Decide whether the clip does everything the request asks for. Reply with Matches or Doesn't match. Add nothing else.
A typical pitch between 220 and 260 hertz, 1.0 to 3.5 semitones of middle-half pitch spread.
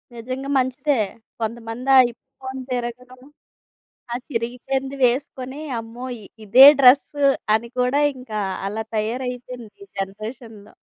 Matches